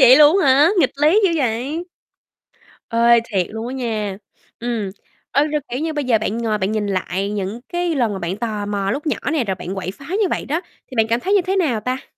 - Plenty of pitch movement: Yes, wide, 6.0 semitones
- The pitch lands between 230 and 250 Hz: Yes, high, 235 Hz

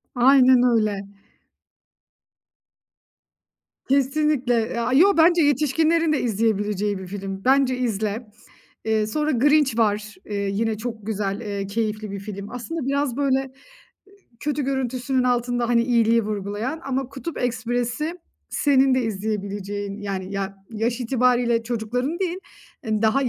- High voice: Yes, high, 235 Hz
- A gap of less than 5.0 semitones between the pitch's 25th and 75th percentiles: Yes, average, 4.2 semitones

